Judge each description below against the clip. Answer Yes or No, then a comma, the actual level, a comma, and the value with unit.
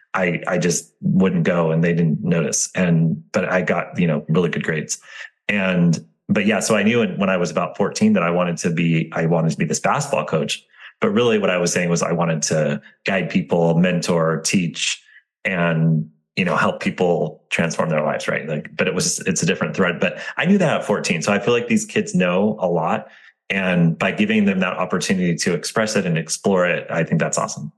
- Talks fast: Yes, fast, 225 wpm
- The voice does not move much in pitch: No, average, 3.5 semitones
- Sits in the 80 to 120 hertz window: Yes, very low, 85 Hz